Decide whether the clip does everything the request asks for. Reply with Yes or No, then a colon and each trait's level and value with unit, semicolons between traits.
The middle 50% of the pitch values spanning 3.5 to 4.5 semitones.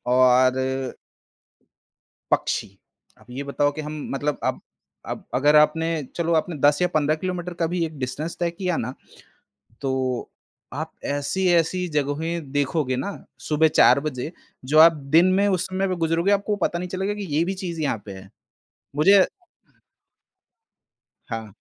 Yes: average, 4.2 semitones